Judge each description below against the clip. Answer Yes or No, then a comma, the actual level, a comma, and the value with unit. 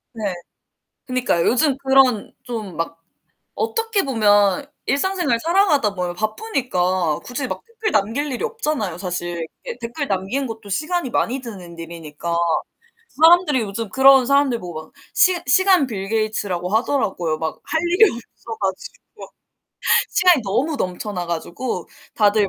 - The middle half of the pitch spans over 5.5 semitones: Yes, wide, 7.1 semitones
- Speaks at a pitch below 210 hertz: No, high, 230 Hz